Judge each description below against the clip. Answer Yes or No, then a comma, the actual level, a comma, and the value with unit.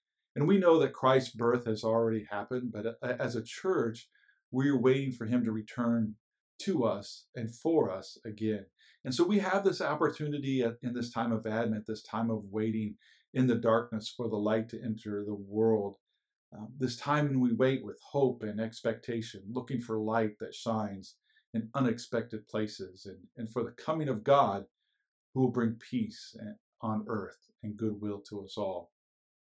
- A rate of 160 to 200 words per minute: Yes, average, 170 wpm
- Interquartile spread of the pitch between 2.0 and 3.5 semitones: Yes, average, 2.8 semitones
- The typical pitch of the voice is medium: No, low, 115 Hz